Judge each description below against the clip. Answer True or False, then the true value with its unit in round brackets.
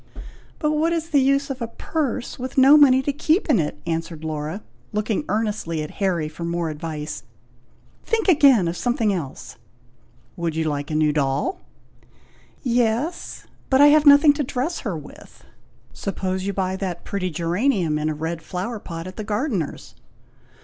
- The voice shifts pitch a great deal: True (8.7 semitones)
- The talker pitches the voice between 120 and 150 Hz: False (200 Hz)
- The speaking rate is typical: True (170 wpm)